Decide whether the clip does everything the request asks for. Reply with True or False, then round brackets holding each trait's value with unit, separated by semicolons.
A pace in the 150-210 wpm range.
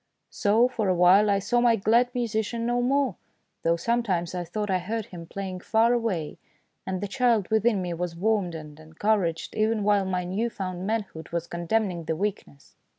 True (185 wpm)